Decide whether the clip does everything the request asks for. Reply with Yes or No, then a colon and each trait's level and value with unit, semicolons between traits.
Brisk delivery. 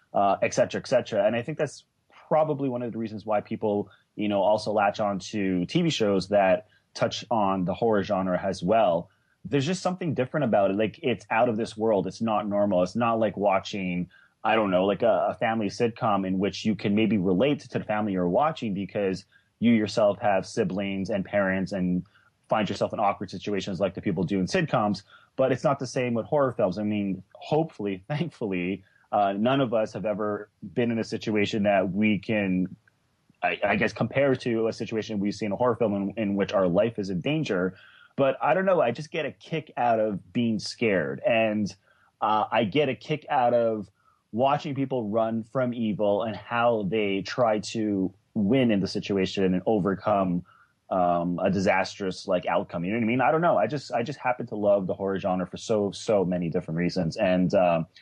Yes: fast, 210 wpm